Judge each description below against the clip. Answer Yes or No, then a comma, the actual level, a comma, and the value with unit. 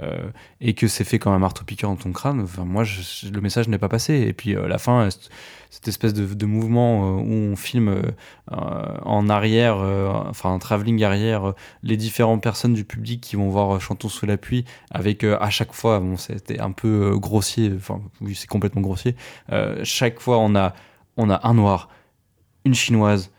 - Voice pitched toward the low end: Yes, low, 105 Hz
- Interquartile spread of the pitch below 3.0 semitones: Yes, narrow, 2.5 semitones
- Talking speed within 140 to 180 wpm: No, average, 215 wpm